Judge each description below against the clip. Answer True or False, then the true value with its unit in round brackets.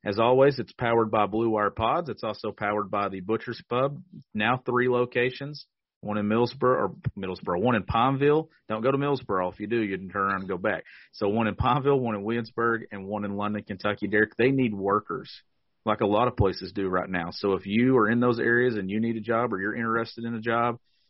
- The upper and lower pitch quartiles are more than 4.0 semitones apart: False (3.2 semitones)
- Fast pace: True (235 wpm)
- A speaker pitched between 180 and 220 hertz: False (115 Hz)